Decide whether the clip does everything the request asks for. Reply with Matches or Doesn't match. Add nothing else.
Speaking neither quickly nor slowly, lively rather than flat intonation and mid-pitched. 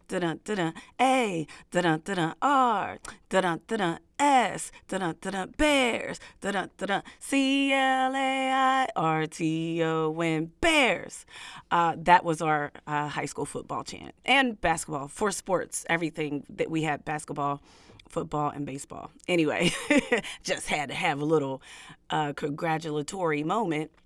Doesn't match